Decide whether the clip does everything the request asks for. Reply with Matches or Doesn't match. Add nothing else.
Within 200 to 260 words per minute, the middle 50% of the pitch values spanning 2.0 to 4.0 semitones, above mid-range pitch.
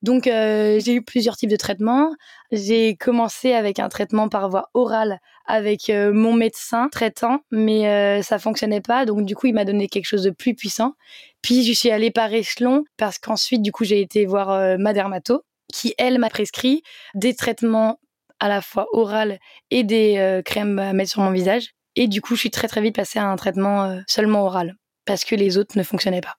Matches